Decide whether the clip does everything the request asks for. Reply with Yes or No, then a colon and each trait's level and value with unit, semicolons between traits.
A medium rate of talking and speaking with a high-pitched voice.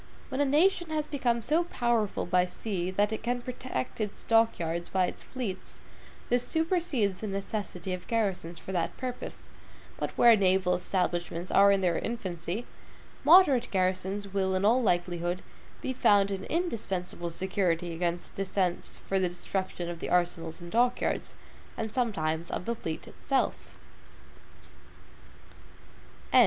Yes: average, 145 wpm; high, 195 Hz